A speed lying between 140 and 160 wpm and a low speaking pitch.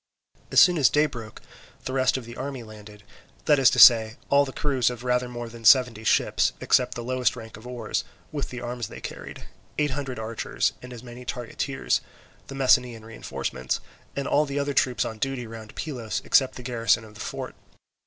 No: average, 200 wpm; low, 125 Hz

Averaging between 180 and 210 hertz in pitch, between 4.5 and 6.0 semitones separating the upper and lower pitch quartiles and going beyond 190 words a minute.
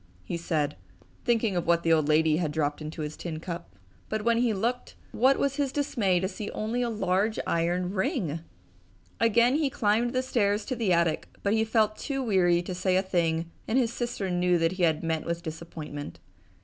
Yes: medium, 185 Hz; wide, 5.5 semitones; average, 200 wpm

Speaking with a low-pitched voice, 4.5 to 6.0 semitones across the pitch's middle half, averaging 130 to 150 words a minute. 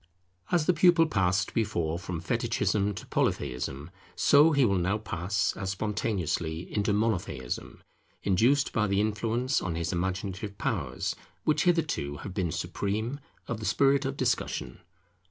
Yes: low, 105 Hz; wide, 5.4 semitones; average, 140 wpm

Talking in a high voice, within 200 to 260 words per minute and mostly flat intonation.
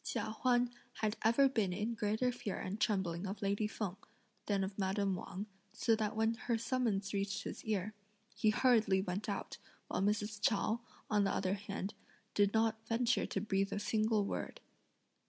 No: high, 210 Hz; average, 175 wpm; narrow, 2.3 semitones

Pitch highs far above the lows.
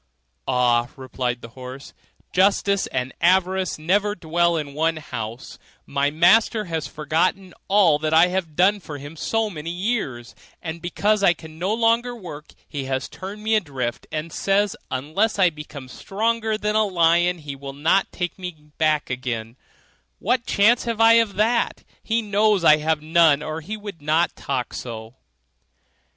Yes: wide, 5.8 semitones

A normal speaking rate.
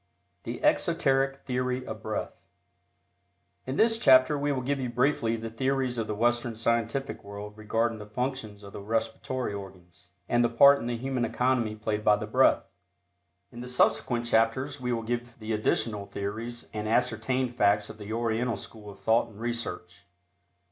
Yes: average, 170 wpm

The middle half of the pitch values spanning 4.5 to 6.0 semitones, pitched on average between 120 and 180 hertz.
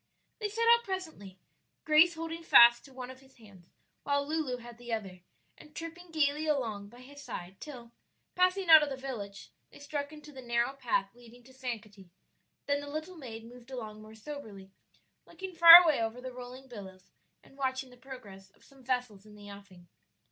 No: average, 5.3 semitones; very high, 255 Hz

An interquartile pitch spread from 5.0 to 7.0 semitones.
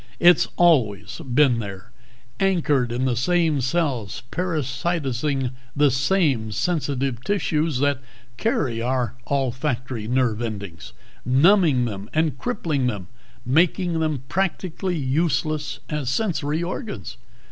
Yes: average, 5.3 semitones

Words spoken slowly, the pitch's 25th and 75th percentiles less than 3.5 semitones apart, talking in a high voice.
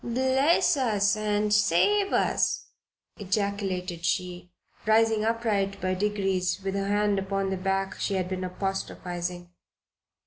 Yes: slow, 125 wpm; narrow, 2.4 semitones; high, 195 Hz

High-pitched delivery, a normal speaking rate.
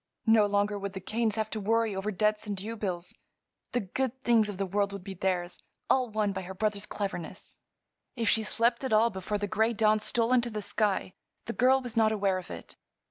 No: high, 210 Hz; fast, 215 wpm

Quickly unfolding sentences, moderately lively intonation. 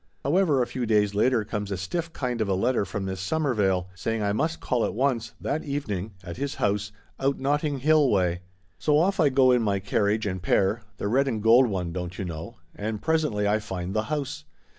No: fast, 215 wpm; wide, 5.8 semitones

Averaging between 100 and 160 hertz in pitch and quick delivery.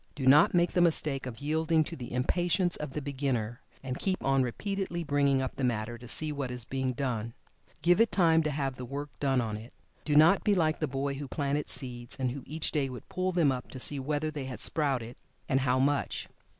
Yes: medium, 140 Hz; fast, 230 wpm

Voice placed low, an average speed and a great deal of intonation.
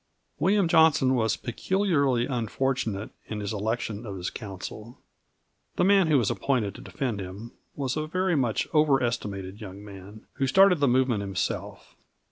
Yes: low, 120 Hz; average, 150 wpm; wide, 5.8 semitones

